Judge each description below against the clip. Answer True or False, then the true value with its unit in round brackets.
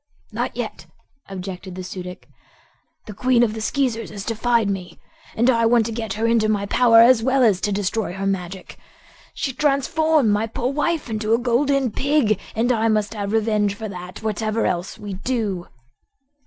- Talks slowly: False (180 wpm)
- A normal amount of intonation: True (3.3 semitones)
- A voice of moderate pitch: False (220 Hz)